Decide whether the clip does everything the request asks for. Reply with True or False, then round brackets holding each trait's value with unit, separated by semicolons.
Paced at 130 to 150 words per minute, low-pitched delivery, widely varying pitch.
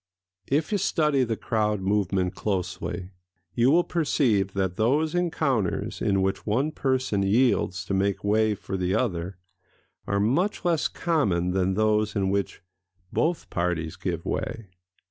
True (145 wpm; 105 Hz; 5.7 semitones)